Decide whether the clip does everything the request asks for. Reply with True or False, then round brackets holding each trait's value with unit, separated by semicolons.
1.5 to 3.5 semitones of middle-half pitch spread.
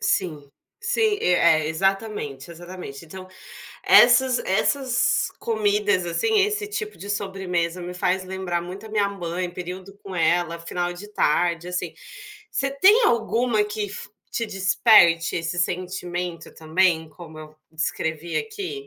False (4.0 semitones)